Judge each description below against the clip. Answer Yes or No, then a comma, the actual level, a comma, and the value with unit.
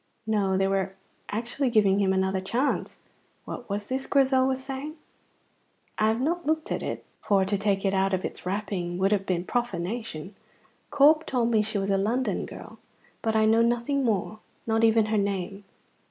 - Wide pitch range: No, average, 4.0 semitones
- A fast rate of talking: No, average, 185 wpm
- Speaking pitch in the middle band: No, high, 215 Hz